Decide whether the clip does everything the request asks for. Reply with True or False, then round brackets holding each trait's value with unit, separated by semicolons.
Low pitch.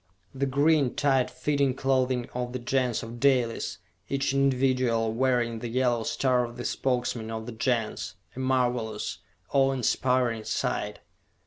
True (125 Hz)